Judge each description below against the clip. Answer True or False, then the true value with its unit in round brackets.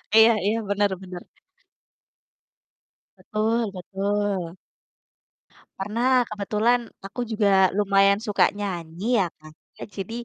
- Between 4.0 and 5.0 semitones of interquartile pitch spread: False (2.5 semitones)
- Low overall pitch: False (205 Hz)